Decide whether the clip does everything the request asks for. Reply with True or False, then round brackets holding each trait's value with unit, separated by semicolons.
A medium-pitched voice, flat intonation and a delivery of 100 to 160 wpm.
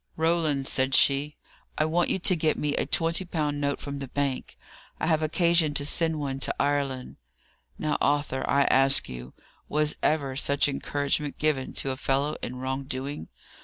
False (145 Hz; 2.3 semitones; 175 wpm)